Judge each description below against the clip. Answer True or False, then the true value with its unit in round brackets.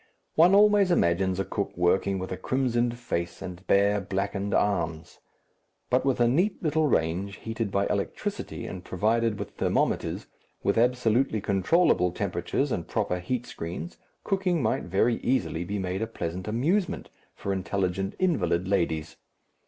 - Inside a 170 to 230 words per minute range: False (145 wpm)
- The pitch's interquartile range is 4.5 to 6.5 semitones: True (5.6 semitones)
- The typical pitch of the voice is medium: False (100 Hz)